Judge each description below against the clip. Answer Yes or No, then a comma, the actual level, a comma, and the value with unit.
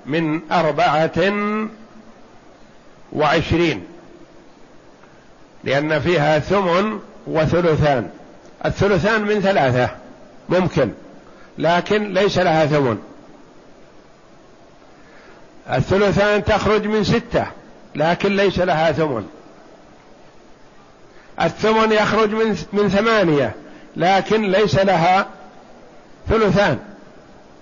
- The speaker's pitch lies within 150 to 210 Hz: Yes, high, 190 Hz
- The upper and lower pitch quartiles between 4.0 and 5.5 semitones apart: Yes, average, 4.9 semitones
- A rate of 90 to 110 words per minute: No, slow, 65 wpm